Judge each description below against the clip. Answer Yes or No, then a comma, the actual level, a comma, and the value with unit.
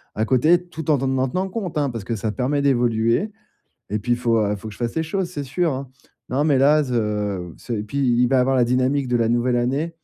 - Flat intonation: No, average, 3.7 semitones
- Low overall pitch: Yes, low, 125 Hz